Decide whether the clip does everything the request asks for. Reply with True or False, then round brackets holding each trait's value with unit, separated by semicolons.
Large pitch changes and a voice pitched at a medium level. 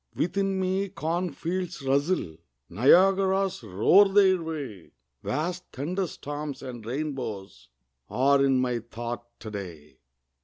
True (7.5 semitones; 145 Hz)